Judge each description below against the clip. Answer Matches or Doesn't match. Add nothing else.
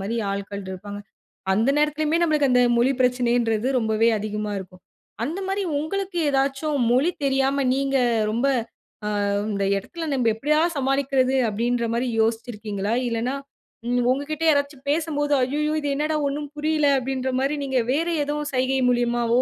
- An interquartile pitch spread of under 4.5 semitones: Matches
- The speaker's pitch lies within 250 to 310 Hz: Matches